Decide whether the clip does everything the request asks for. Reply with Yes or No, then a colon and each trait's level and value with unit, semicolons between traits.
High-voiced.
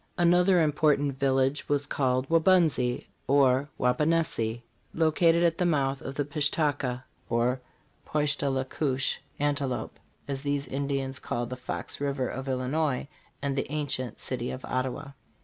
No: medium, 140 Hz